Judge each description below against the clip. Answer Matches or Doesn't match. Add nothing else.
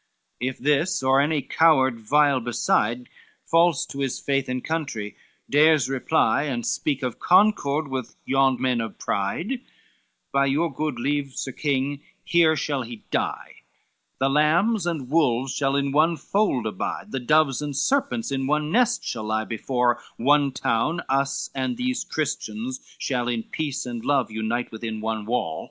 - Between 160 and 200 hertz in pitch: Doesn't match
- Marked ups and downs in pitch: Doesn't match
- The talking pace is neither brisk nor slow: Matches